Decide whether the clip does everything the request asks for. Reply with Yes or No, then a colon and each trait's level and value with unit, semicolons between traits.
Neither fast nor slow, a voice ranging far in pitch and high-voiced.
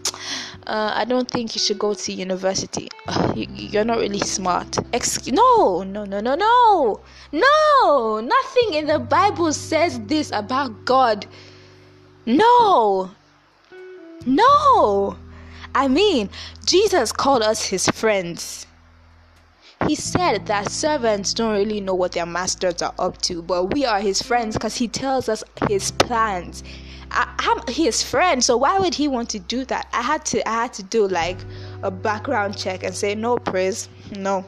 Yes: average, 160 wpm; wide, 7.5 semitones; high, 215 Hz